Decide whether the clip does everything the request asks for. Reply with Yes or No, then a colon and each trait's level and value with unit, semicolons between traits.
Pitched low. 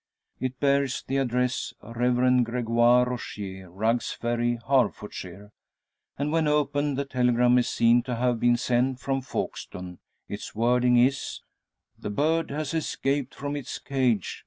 Yes: low, 125 Hz